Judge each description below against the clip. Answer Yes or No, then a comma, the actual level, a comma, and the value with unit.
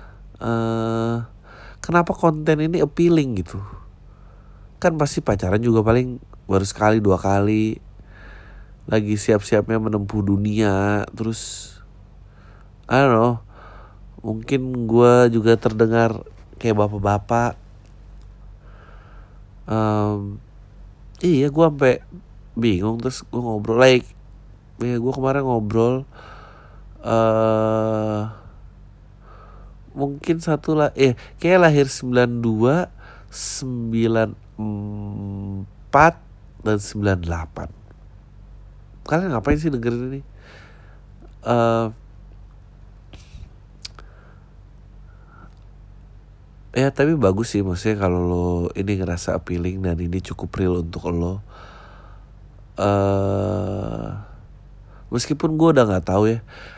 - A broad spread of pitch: No, average, 3.4 semitones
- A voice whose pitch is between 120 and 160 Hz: No, low, 110 Hz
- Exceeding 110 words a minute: No, average, 90 wpm